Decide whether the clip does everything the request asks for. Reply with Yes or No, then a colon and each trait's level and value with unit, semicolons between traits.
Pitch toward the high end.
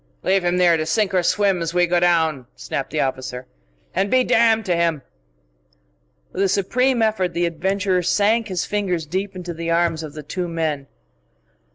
No: medium, 175 Hz